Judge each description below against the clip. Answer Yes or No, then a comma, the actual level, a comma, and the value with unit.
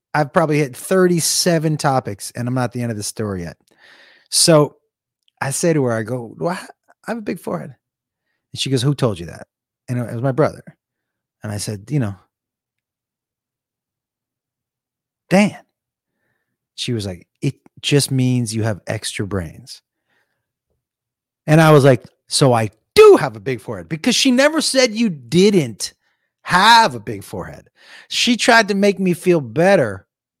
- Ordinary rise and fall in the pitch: No, wide, 6.4 semitones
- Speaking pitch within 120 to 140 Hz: Yes, low, 135 Hz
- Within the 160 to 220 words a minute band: Yes, average, 165 wpm